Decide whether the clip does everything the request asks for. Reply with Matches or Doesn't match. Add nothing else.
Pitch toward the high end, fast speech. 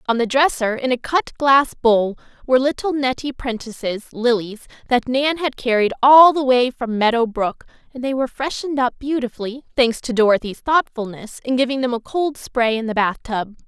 Doesn't match